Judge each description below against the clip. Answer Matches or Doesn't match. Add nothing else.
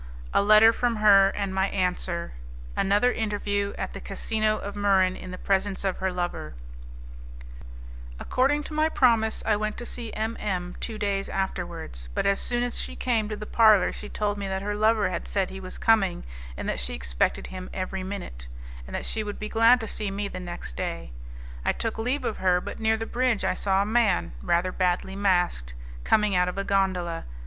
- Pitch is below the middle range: Doesn't match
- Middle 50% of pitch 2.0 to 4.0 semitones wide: Matches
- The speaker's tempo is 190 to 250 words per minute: Matches